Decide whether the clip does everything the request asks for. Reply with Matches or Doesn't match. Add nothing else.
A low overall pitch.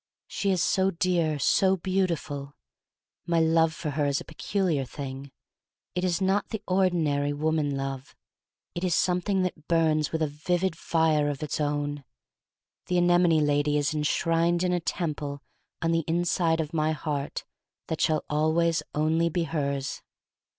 Doesn't match